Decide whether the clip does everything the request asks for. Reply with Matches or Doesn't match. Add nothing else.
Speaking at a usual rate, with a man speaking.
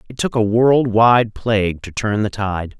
Matches